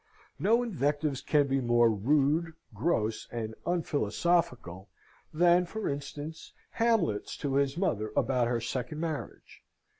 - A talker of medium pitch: Yes, medium, 145 Hz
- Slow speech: Yes, slow, 120 wpm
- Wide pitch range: Yes, wide, 6.0 semitones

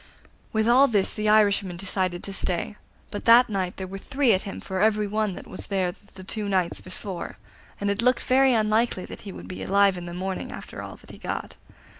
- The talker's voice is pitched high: Yes, high, 200 Hz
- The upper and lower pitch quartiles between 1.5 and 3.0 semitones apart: Yes, narrow, 2.6 semitones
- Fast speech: Yes, fast, 220 wpm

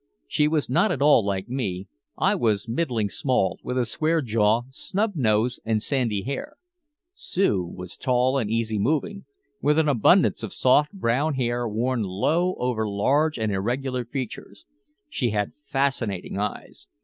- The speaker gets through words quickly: No, average, 155 wpm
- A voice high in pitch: No, low, 125 Hz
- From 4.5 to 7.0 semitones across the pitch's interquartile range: Yes, average, 5.1 semitones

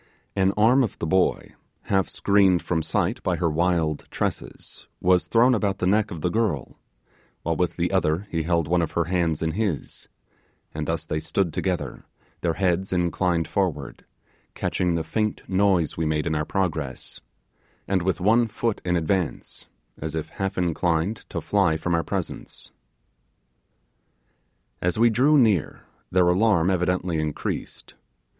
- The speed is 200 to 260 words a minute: No, average, 155 wpm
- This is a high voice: No, very low, 90 Hz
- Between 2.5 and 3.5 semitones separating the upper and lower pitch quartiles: Yes, average, 3.1 semitones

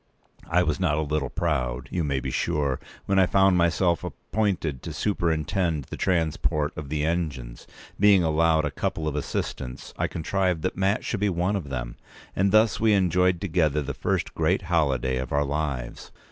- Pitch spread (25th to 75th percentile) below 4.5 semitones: Yes, average, 4.0 semitones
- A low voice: Yes, very low, 80 Hz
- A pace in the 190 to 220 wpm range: No, average, 180 wpm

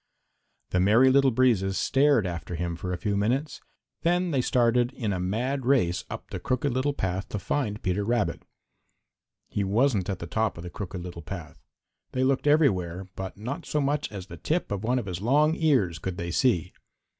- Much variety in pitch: Yes, wide, 6.4 semitones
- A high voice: No, low, 105 Hz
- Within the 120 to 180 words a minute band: No, average, 195 wpm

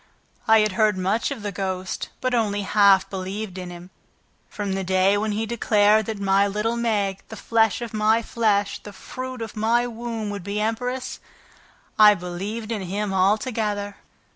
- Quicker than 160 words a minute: Yes, average, 170 wpm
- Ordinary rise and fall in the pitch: No, narrow, 2.3 semitones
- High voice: Yes, high, 210 Hz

